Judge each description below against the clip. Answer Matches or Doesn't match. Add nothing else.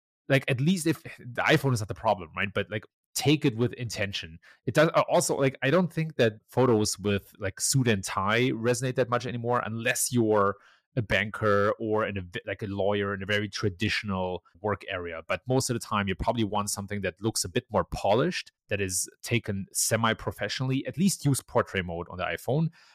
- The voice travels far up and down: Doesn't match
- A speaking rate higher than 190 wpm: Matches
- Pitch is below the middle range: Matches